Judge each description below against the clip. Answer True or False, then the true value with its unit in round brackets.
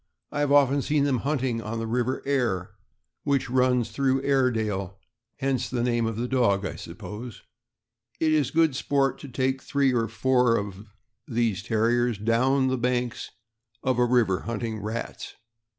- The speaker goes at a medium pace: True (160 wpm)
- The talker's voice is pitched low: True (125 Hz)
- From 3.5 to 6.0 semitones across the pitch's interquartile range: False (2.8 semitones)